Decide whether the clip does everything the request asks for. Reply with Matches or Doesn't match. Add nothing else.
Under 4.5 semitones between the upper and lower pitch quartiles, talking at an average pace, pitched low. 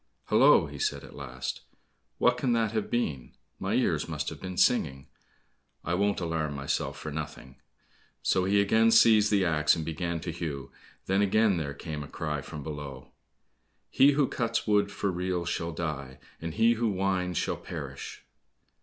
Doesn't match